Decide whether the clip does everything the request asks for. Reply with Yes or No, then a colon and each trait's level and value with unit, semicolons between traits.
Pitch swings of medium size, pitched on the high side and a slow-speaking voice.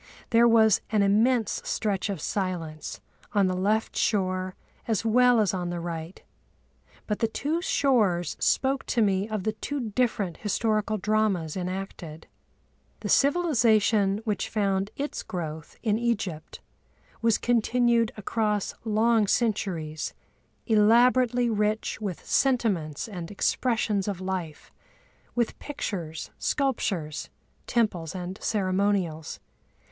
Yes: average, 3.7 semitones; high, 210 Hz; slow, 115 wpm